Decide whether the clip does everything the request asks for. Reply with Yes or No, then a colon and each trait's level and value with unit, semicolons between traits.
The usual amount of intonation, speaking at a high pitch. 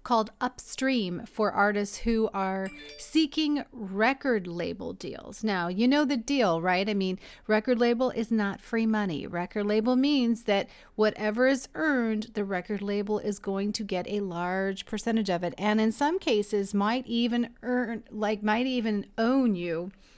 Yes: average, 3.3 semitones; high, 215 Hz